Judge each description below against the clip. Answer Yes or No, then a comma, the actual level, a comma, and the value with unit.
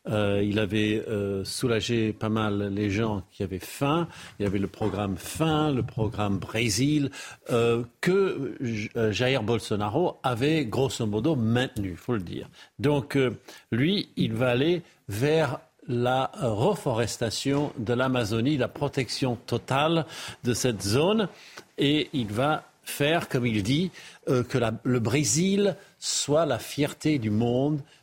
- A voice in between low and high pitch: No, low, 125 Hz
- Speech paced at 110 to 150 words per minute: Yes, slow, 145 wpm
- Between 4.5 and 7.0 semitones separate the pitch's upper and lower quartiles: Yes, average, 5.1 semitones